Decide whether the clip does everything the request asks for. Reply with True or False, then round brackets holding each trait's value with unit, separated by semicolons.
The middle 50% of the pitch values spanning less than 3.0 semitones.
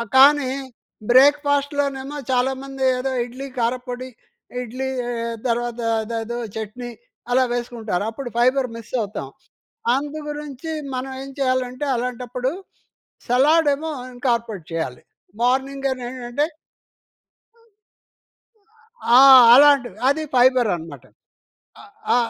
True (2.4 semitones)